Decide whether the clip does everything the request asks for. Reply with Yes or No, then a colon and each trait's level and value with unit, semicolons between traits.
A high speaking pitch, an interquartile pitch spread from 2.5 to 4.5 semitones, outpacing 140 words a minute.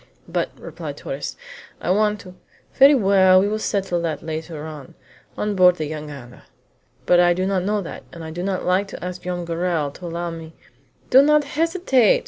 No: medium, 180 Hz; average, 3.7 semitones; average, 200 wpm